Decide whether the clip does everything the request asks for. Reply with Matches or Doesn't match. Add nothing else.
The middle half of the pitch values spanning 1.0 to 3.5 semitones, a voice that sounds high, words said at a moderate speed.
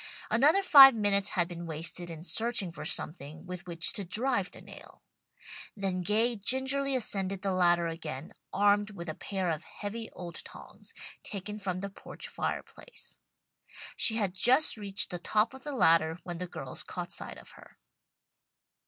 Doesn't match